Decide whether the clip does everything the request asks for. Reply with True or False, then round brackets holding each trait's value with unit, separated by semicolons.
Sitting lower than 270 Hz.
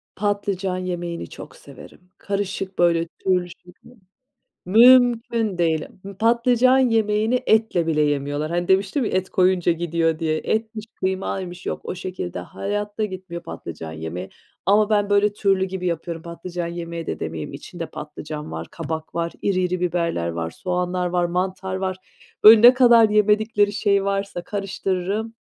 True (185 Hz)